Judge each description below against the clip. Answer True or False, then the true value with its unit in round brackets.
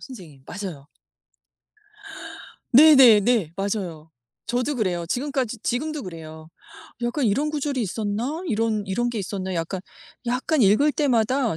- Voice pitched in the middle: False (225 Hz)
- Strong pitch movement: True (5.9 semitones)